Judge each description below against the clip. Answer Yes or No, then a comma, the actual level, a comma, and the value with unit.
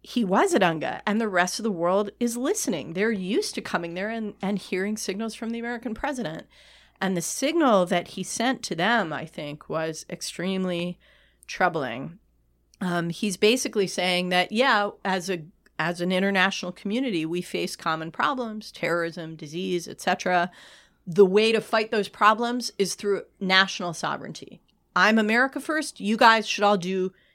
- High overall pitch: Yes, high, 195 Hz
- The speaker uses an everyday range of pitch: Yes, average, 4.0 semitones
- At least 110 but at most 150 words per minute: No, average, 165 wpm